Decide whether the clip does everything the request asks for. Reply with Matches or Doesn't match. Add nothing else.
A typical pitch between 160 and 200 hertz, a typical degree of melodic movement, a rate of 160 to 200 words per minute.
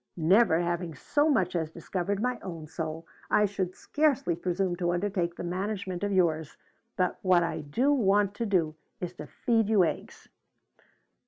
Matches